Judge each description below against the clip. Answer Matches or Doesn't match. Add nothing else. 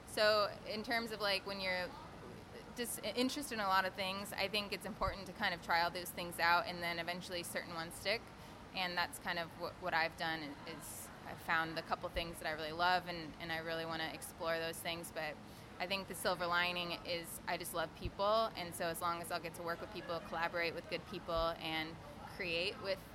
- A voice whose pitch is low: Doesn't match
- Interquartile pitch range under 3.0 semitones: Matches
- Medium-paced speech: Doesn't match